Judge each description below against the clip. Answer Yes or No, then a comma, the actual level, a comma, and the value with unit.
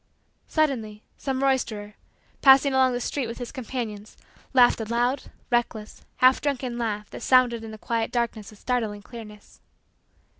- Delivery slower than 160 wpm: Yes, average, 150 wpm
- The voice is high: Yes, high, 240 Hz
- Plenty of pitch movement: No, average, 3.0 semitones